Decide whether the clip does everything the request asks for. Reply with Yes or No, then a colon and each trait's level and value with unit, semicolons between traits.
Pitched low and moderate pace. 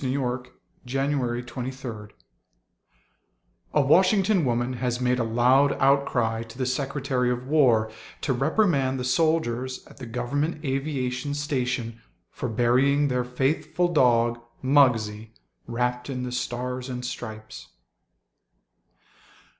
No: low, 125 Hz; slow, 120 wpm